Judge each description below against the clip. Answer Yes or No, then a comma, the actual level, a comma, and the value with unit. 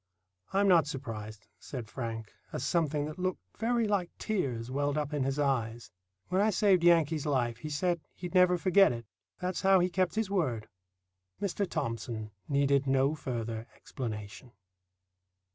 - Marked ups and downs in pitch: Yes, wide, 7.3 semitones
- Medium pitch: Yes, medium, 145 Hz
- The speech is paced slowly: No, average, 155 wpm